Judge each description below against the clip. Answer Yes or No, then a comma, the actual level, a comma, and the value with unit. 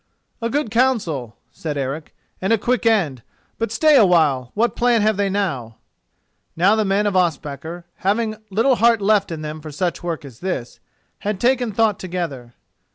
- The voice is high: Yes, high, 195 Hz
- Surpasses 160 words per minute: Yes, average, 175 wpm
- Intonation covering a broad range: Yes, wide, 6.4 semitones